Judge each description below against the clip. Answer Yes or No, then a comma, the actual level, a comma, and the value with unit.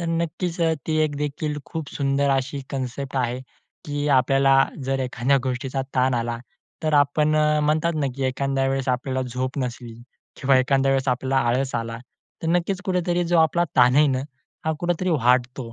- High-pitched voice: No, low, 135 Hz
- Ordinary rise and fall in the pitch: Yes, average, 3.1 semitones